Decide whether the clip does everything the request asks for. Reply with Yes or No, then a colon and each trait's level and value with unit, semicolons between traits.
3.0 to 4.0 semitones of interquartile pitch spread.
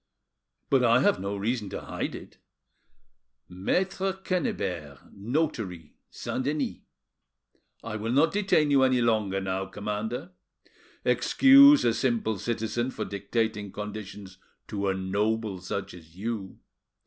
No: average, 4.8 semitones